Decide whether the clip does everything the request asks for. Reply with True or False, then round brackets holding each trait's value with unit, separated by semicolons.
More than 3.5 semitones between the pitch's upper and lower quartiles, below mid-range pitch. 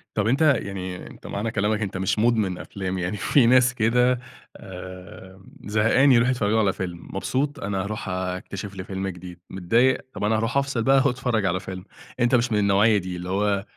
True (4.1 semitones; 105 Hz)